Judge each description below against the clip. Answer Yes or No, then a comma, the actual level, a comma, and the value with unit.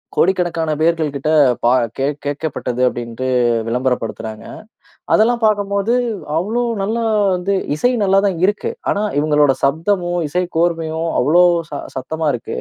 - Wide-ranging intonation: Yes, wide, 5.9 semitones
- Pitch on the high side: No, medium, 165 Hz